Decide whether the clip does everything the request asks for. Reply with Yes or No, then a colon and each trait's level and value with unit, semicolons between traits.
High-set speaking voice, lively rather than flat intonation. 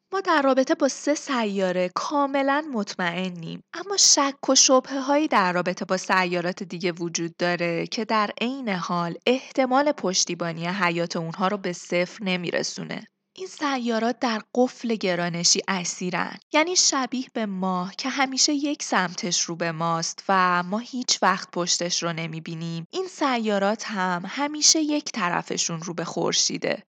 Yes: high, 200 Hz; wide, 7.2 semitones